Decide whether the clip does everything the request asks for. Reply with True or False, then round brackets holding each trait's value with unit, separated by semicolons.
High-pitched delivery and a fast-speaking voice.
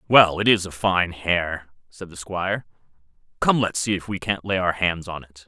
False (90 Hz; 220 wpm)